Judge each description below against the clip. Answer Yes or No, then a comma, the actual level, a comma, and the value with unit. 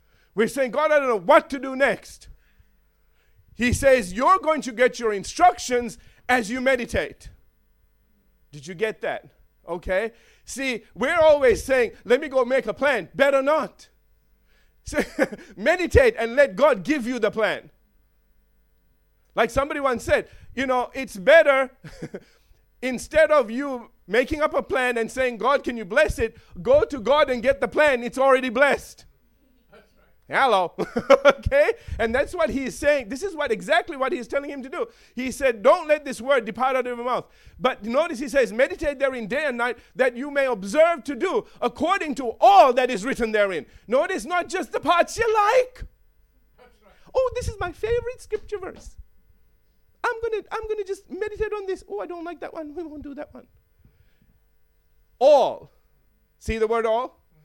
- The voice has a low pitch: No, very high, 275 Hz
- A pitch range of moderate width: Yes, average, 4.9 semitones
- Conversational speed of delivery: Yes, average, 175 wpm